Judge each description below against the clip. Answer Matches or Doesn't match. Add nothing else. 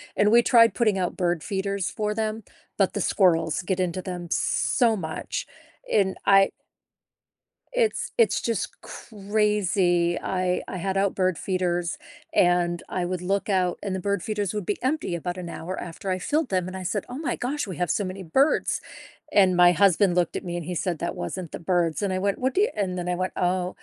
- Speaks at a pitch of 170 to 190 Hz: Matches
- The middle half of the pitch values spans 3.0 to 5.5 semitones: Doesn't match